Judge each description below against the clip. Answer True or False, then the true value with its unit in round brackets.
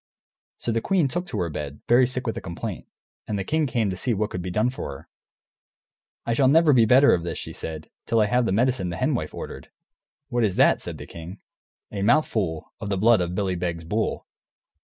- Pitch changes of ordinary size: False (5.8 semitones)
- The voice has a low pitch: True (105 Hz)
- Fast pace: True (230 wpm)